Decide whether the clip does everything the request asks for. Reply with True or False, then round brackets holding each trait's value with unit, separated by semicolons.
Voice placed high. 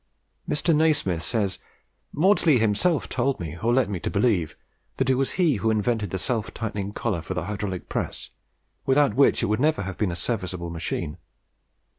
False (110 Hz)